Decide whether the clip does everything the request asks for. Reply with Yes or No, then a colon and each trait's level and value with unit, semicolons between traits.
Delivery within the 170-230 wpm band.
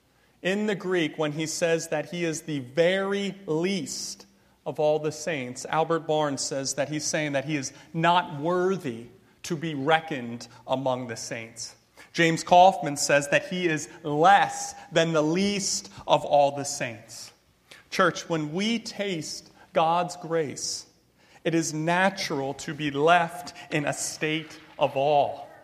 No: average, 150 wpm